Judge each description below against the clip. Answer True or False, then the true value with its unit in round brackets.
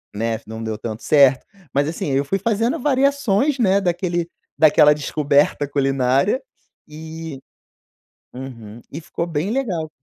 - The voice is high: False (155 Hz)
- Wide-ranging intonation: True (6.3 semitones)